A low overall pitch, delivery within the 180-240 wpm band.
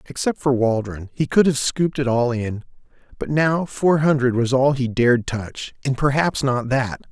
Yes: low, 130 Hz; average, 185 wpm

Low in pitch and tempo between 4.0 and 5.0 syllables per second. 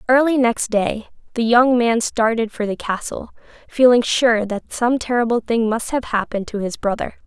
No: high, 230 Hz; 4.9 syllables/s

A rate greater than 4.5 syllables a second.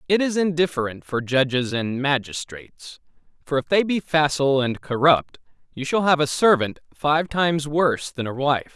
Yes: 5.0 syllables/s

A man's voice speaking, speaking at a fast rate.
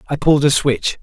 Yes: male; fast, 235 wpm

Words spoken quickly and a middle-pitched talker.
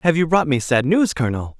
Yes: fast, 265 wpm; medium, 150 Hz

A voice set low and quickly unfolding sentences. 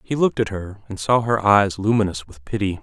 Yes: low, 100 Hz; fast, 235 wpm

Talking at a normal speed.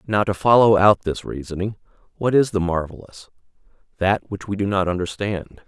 Yes: average, 160 wpm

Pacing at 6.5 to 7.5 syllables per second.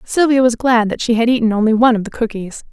Yes: 6.7 syllables/s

